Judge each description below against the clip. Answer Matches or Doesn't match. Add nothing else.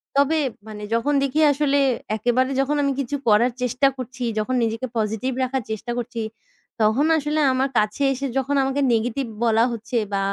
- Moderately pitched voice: Doesn't match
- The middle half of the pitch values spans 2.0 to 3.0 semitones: Doesn't match